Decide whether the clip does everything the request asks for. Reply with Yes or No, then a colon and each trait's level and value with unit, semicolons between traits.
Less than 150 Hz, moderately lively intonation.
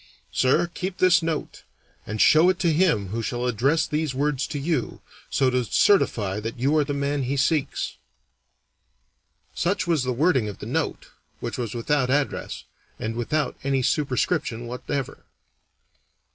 Yes: medium, 140 Hz; average, 4.4 semitones